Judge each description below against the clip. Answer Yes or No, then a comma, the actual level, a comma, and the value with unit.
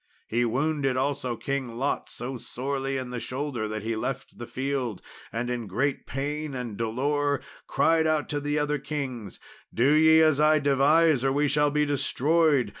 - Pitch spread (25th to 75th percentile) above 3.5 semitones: No, average, 3.1 semitones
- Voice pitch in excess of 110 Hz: Yes, low, 135 Hz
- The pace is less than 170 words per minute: No, average, 175 wpm